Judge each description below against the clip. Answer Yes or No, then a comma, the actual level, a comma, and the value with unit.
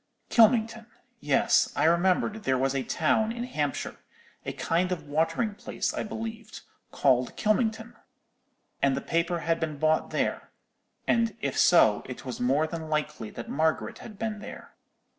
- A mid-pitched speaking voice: Yes, medium, 170 Hz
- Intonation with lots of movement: Yes, wide, 6.8 semitones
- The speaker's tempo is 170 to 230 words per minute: No, average, 140 wpm